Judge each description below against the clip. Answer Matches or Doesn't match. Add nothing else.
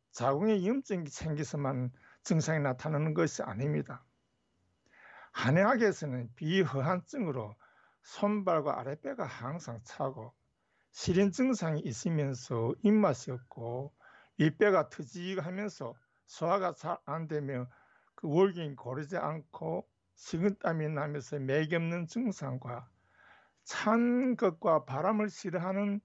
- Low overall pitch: Doesn't match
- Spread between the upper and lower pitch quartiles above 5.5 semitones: Matches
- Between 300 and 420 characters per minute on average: Doesn't match